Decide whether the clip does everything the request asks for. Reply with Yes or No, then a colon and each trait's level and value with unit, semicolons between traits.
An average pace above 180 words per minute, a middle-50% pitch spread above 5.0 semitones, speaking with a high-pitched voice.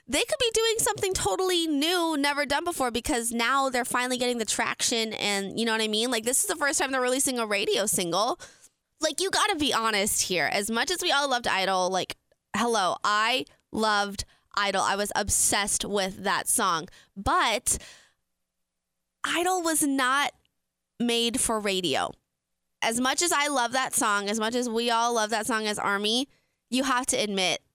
Yes: average, 190 wpm; wide, 5.4 semitones; high, 235 Hz